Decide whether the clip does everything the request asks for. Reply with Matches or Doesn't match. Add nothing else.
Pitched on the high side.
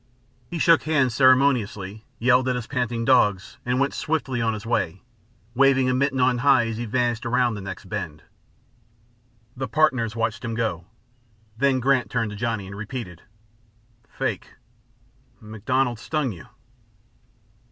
Doesn't match